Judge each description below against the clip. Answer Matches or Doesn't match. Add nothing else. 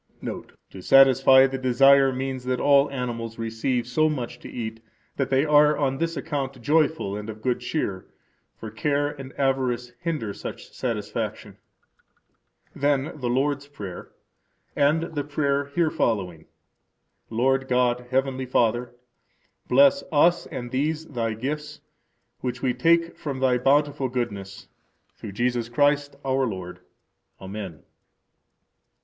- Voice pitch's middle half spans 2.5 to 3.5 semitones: Matches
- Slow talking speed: Matches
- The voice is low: Matches